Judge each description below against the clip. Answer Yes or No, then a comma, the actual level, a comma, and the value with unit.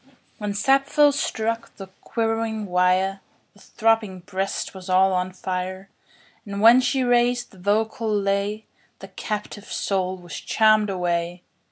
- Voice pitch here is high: Yes, high, 205 Hz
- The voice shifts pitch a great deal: No, average, 3.2 semitones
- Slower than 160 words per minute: Yes, average, 140 wpm